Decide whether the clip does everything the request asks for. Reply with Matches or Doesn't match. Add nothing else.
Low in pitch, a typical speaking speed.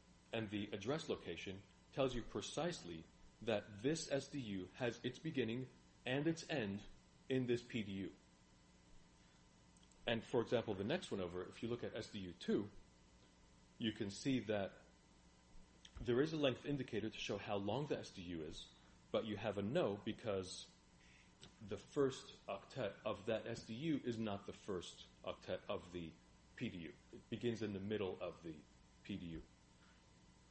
Matches